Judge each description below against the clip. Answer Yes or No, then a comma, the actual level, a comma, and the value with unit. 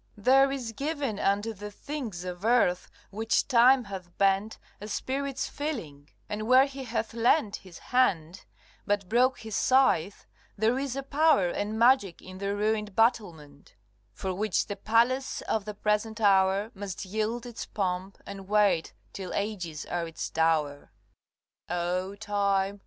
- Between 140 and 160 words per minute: Yes, average, 150 wpm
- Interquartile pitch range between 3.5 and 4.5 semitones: Yes, average, 4.0 semitones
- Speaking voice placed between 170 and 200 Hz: No, high, 210 Hz